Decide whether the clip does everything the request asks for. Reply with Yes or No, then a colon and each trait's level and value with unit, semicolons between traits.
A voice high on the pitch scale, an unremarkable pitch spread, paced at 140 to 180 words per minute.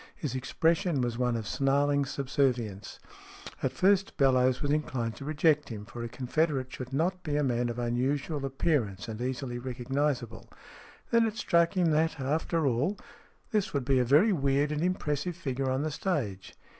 No: medium, 140 Hz; average, 4.0 semitones; average, 170 wpm